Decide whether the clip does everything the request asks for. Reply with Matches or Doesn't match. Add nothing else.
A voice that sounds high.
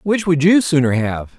Doesn't match